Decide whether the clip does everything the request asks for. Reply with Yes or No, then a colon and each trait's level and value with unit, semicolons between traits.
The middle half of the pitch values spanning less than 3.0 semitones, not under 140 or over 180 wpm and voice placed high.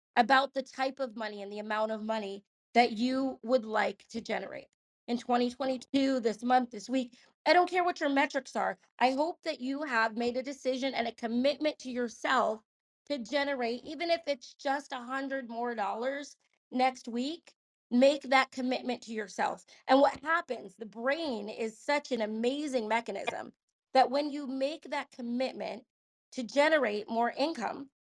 No: average, 3.3 semitones; average, 170 wpm; very high, 255 Hz